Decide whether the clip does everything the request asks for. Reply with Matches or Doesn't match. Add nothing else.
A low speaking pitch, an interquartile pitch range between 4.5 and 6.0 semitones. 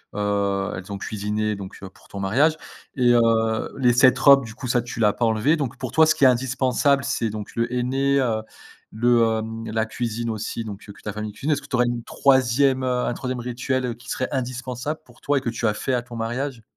Doesn't match